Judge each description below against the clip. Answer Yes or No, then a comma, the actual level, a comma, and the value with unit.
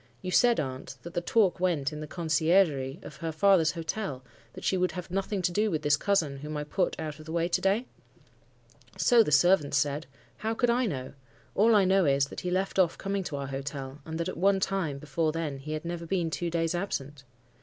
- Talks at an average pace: No, fast, 230 wpm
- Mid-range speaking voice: Yes, medium, 165 Hz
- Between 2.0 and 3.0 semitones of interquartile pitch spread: No, average, 4.5 semitones